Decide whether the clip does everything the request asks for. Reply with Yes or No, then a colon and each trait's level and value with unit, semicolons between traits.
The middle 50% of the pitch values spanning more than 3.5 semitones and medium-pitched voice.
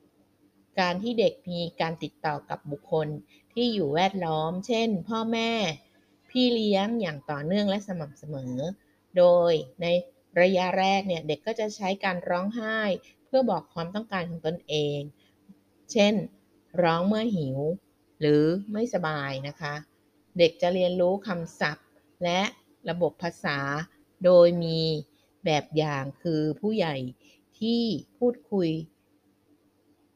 Yes: average, 4.7 semitones; medium, 175 Hz